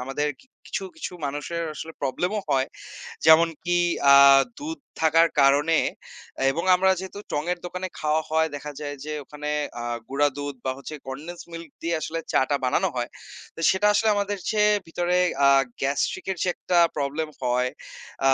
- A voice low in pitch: No, medium, 160 Hz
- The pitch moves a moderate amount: Yes, average, 3.7 semitones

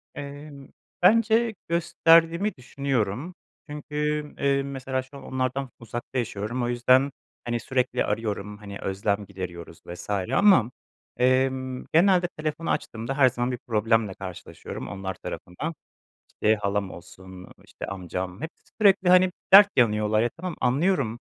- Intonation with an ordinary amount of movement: No, wide, 6.1 semitones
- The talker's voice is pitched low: Yes, low, 125 Hz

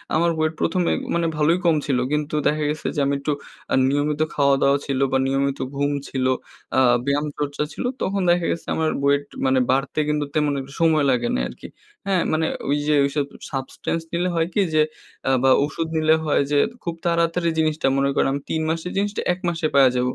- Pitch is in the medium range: Yes, medium, 150 Hz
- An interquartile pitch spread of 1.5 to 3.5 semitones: Yes, average, 2.9 semitones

